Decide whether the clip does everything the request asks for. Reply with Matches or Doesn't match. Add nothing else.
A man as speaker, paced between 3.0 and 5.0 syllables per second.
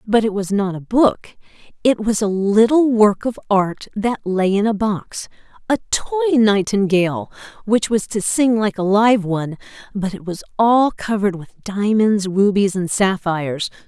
Doesn't match